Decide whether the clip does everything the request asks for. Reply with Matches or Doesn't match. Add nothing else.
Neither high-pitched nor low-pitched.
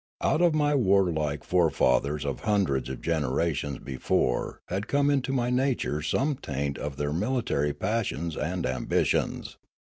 Doesn't match